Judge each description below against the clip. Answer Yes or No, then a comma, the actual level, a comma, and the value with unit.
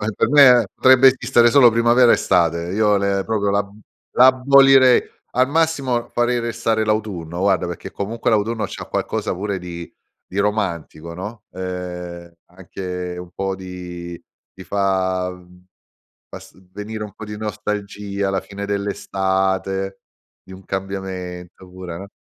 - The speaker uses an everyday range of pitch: Yes, average, 3.5 semitones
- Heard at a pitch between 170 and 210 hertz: No, low, 100 Hz